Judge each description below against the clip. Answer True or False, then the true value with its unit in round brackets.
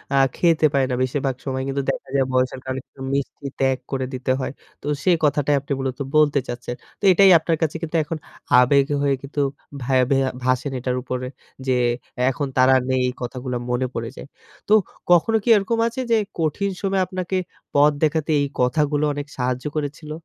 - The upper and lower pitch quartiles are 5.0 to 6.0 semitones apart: False (3.4 semitones)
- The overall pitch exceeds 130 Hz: True (140 Hz)